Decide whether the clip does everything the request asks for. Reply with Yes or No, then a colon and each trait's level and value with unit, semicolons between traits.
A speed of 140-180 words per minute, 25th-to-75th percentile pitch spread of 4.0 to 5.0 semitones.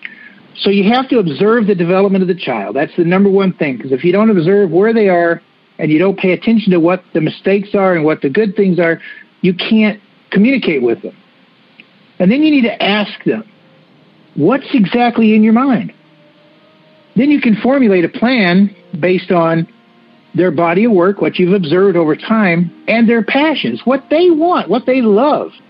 No: average, 190 wpm; average, 4.3 semitones